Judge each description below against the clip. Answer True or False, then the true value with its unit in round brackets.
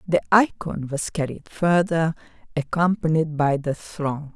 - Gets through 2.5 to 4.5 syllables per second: True (4.1 syllables/s)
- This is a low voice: False (160 Hz)